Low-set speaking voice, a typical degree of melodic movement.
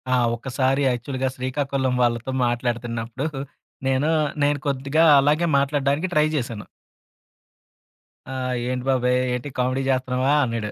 No: low, 130 Hz; narrow, 2.2 semitones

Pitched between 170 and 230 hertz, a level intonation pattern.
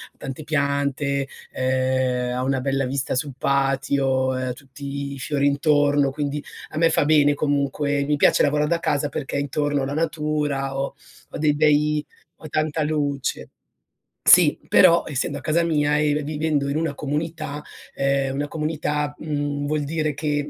No: medium, 145 Hz; narrow, 1.6 semitones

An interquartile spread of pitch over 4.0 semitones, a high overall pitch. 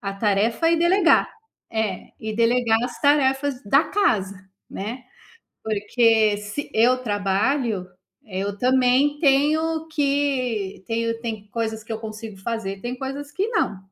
Yes: average, 4.9 semitones; high, 230 Hz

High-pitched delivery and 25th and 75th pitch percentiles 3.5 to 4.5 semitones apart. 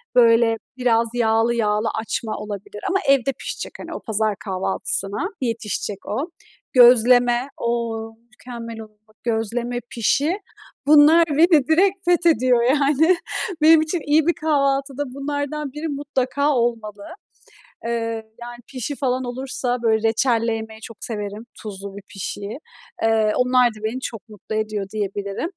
Yes: high, 235 Hz; average, 3.8 semitones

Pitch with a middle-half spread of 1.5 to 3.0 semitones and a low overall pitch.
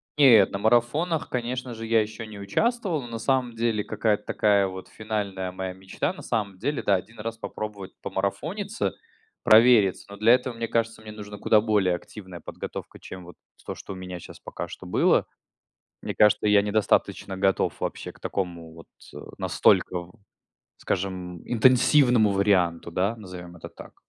No: average, 3.6 semitones; low, 105 Hz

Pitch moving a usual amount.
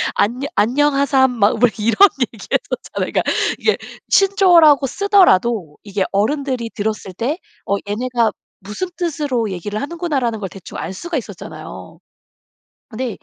No: wide, 5.8 semitones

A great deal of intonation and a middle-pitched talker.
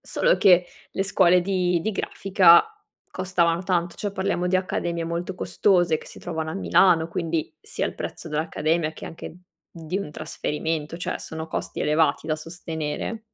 No: narrow, 2.5 semitones; medium, 170 Hz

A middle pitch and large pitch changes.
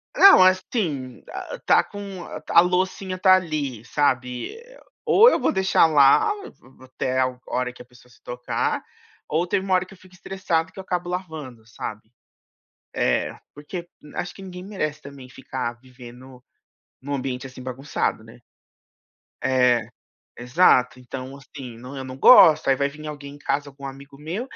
Yes: medium, 145 Hz; wide, 6.1 semitones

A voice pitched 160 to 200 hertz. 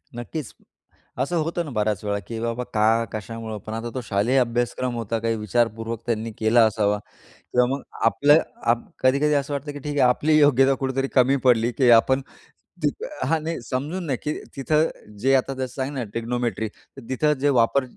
No: low, 125 Hz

